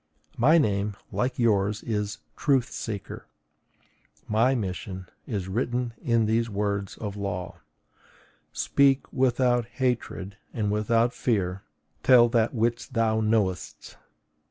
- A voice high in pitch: No, low, 110 Hz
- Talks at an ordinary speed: No, slow, 115 wpm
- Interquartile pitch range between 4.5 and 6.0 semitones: No, average, 3.2 semitones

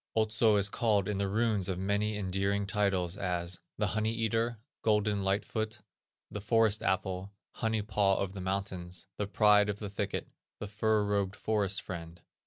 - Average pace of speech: Yes, average, 170 wpm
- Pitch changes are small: Yes, narrow, 1.9 semitones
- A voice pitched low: Yes, low, 100 Hz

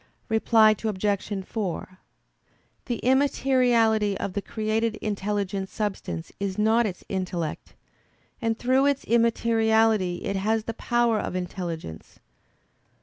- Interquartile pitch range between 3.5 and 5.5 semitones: No, average, 3.0 semitones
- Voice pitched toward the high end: Yes, high, 215 Hz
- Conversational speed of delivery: No, slow, 110 wpm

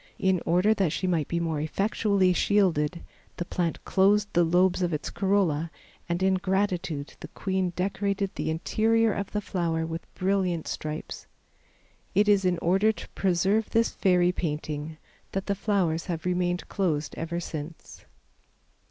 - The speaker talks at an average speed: Yes, average, 150 wpm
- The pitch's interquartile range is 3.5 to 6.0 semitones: No, average, 3.0 semitones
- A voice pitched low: No, medium, 180 Hz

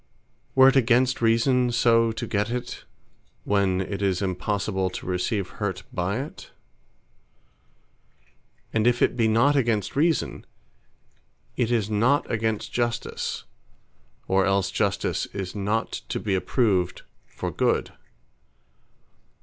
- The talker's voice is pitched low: Yes, low, 110 Hz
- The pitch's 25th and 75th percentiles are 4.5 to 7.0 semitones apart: No, average, 3.8 semitones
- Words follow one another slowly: Yes, slow, 120 wpm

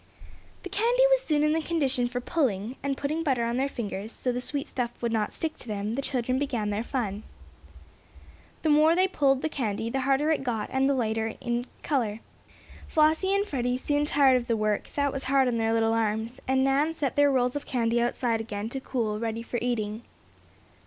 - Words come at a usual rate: No, fast, 210 wpm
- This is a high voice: Yes, very high, 255 Hz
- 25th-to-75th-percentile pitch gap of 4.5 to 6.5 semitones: No, average, 4.0 semitones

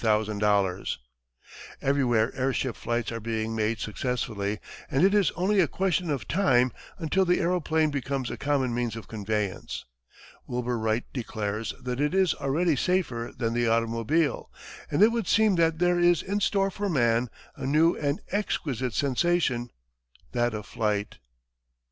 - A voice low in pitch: Yes, low, 130 Hz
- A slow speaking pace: No, average, 150 wpm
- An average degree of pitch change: No, wide, 7.0 semitones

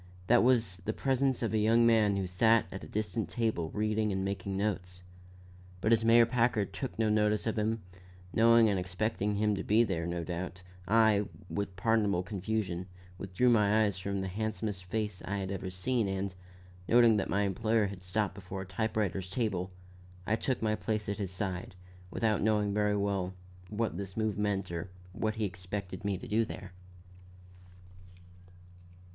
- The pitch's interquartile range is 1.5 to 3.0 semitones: Yes, average, 2.7 semitones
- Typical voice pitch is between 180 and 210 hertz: No, low, 105 Hz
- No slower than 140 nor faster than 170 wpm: No, average, 180 wpm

